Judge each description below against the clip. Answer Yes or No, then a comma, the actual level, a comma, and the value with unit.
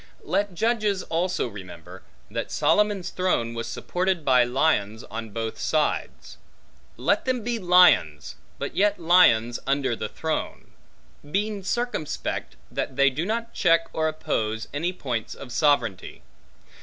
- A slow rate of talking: Yes, slow, 130 wpm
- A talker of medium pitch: Yes, medium, 155 Hz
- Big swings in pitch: Yes, wide, 8.4 semitones